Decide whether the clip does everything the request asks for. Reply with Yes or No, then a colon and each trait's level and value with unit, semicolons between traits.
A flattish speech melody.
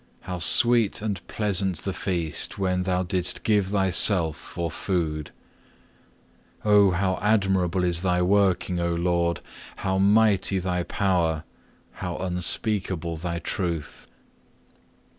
Yes: narrow, 2.2 semitones